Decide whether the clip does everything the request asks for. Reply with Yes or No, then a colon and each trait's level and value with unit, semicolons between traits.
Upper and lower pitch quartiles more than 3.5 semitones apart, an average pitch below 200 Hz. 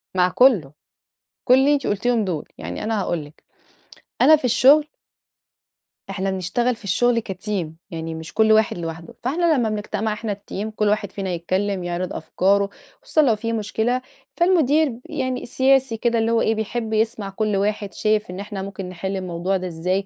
No: average, 4.3 semitones; high, 210 Hz